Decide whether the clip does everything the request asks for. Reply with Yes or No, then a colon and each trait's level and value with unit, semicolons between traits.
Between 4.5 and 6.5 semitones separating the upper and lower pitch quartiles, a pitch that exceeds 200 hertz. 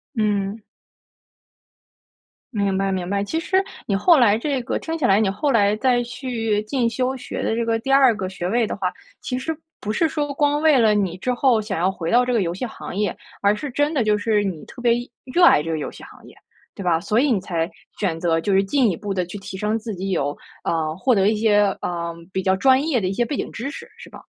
Yes: average, 4.8 semitones; high, 215 Hz